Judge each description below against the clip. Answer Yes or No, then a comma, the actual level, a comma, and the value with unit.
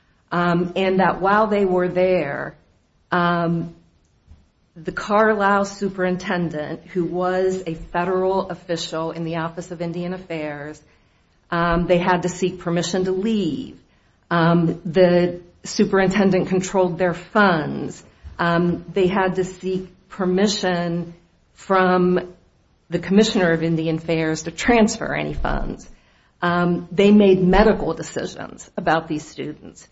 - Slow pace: Yes, slow, 120 wpm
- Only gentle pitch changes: Yes, narrow, 2.1 semitones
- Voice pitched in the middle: Yes, medium, 175 Hz